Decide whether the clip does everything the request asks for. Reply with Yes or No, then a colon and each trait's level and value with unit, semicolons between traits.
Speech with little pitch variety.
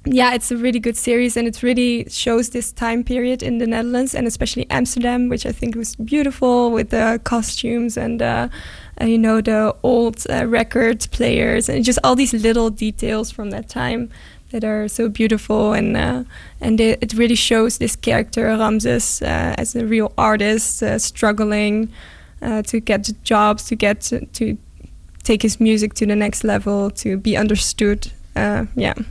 Yes: narrow, 2.0 semitones